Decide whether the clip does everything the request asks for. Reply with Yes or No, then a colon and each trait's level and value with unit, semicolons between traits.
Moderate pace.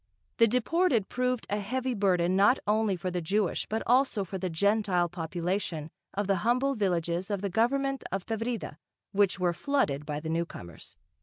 Yes: average, 170 wpm